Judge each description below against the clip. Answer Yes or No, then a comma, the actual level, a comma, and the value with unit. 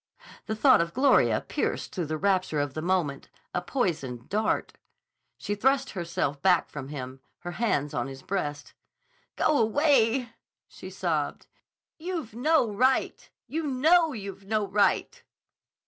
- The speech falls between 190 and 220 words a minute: No, average, 140 wpm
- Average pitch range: No, wide, 8.7 semitones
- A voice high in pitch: Yes, high, 200 Hz